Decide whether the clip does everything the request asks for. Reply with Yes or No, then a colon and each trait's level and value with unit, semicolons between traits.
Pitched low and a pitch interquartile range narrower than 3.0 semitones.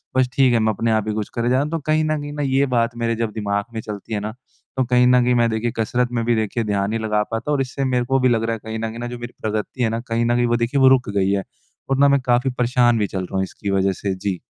Yes: low, 115 Hz; narrow, 2.6 semitones